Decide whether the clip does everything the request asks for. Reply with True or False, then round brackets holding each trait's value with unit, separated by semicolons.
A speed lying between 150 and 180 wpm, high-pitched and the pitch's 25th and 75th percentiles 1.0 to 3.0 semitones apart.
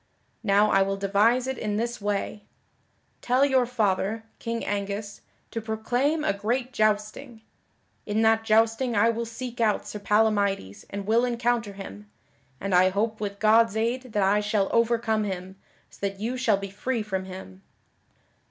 True (160 wpm; 215 Hz; 2.7 semitones)